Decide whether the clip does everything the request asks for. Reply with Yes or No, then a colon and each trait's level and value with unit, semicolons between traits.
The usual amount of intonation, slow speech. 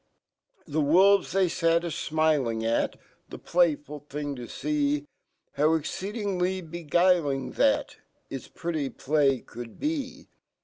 Yes: average, 3.9 semitones; slow, 120 wpm